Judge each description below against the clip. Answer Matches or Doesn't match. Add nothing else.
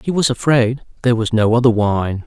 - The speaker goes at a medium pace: Doesn't match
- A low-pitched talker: Matches